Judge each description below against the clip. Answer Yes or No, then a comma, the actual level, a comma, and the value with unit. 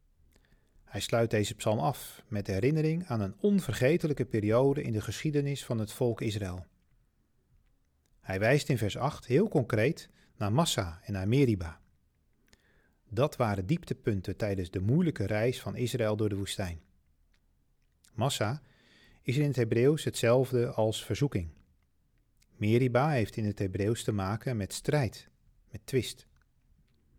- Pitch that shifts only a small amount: No, average, 5.1 semitones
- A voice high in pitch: No, low, 110 Hz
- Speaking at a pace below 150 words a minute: Yes, slow, 135 wpm